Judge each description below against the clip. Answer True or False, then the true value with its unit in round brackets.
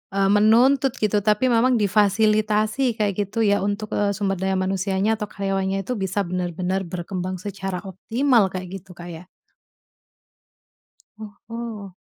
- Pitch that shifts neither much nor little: False (2.2 semitones)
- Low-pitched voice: False (200 Hz)